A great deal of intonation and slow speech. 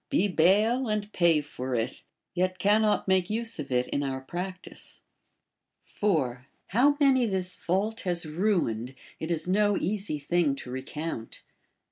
No: wide, 6.2 semitones; average, 145 wpm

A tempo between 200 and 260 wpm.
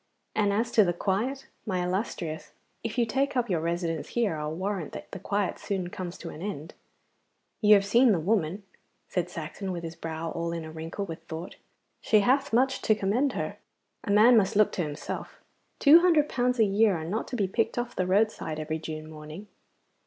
Yes: fast, 205 wpm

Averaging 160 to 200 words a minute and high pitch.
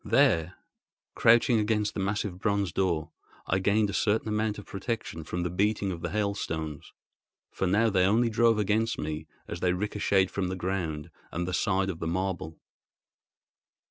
No: average, 170 wpm; very low, 95 Hz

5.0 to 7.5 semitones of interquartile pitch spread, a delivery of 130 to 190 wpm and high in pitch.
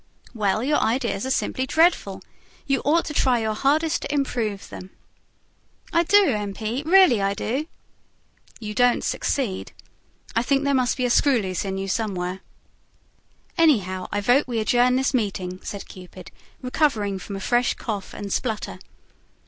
Yes: average, 5.3 semitones; average, 160 wpm; high, 235 Hz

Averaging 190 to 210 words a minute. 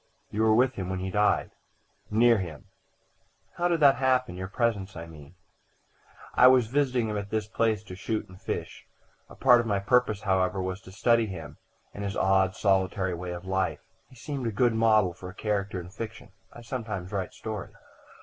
Yes: average, 195 wpm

